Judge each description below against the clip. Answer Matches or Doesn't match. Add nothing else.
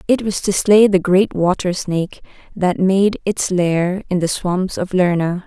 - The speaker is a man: Doesn't match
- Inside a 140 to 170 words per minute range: Doesn't match